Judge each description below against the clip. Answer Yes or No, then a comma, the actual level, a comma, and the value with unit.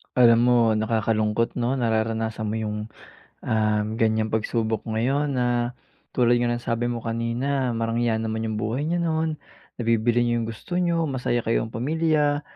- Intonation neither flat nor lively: No, narrow, 2.1 semitones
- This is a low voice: Yes, low, 115 Hz